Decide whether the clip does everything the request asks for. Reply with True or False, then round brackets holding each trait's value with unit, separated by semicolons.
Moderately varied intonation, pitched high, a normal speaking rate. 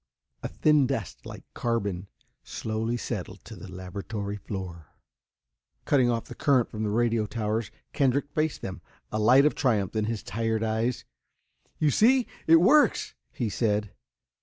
False (3.8 semitones; 115 Hz; 150 wpm)